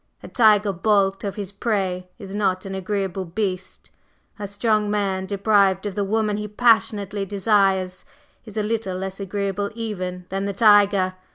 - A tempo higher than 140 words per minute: Yes, average, 160 wpm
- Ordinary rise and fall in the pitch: No, narrow, 1.7 semitones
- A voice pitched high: Yes, high, 200 Hz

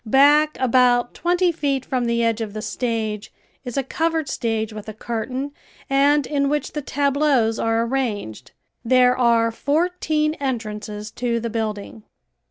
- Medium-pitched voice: No, high, 245 Hz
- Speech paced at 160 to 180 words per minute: No, average, 150 wpm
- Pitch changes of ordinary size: Yes, average, 4.0 semitones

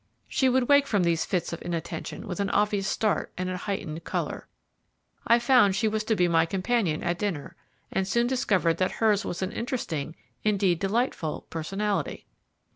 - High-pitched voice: Yes, high, 195 Hz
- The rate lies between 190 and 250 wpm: No, average, 175 wpm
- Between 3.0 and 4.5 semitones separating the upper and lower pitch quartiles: Yes, average, 4.2 semitones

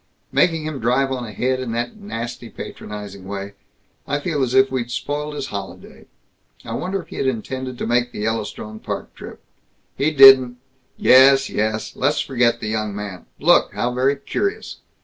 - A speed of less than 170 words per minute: No, average, 175 wpm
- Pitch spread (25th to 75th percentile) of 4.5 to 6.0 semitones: No, average, 3.7 semitones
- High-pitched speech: No, low, 125 Hz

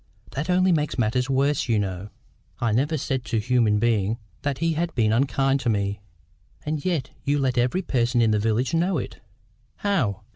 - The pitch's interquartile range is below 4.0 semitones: No, average, 4.9 semitones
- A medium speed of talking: Yes, average, 185 wpm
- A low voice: Yes, low, 125 Hz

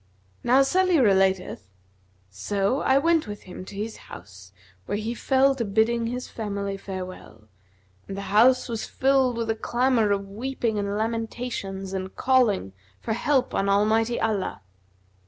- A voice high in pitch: Yes, high, 220 Hz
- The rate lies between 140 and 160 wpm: Yes, average, 150 wpm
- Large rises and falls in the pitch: No, average, 4.1 semitones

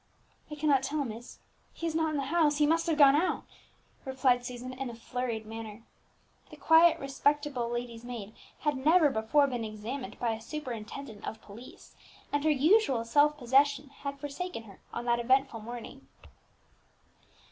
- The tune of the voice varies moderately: Yes, average, 3.8 semitones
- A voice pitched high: Yes, very high, 265 Hz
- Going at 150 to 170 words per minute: Yes, average, 165 wpm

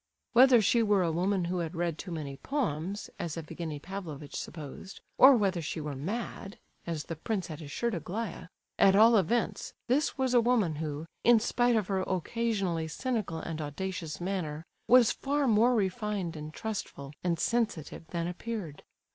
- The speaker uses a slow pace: No, average, 165 wpm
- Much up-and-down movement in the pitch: Yes, wide, 5.9 semitones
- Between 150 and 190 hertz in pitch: Yes, medium, 185 Hz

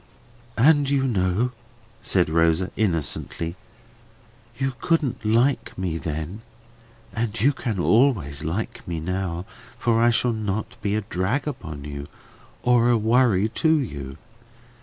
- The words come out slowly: Yes, slow, 130 wpm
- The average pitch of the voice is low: Yes, low, 110 Hz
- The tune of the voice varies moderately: No, wide, 6.3 semitones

